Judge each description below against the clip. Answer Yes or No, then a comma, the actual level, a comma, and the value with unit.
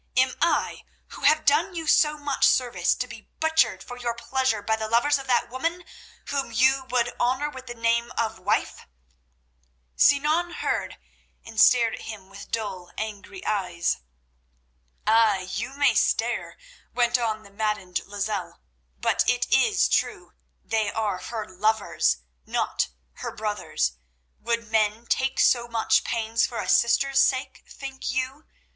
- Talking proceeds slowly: No, average, 150 wpm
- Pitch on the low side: No, high, 235 Hz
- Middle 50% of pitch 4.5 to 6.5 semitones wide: No, average, 3.8 semitones